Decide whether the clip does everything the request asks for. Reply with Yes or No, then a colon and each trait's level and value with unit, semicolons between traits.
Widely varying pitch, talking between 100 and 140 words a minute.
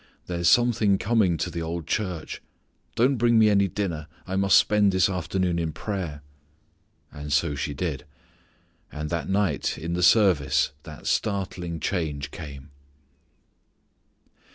No: average, 4.4 semitones; slow, 135 wpm